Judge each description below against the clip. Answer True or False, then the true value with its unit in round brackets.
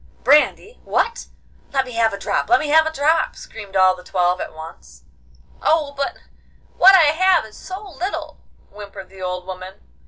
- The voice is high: True (250 Hz)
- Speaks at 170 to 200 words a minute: True (180 wpm)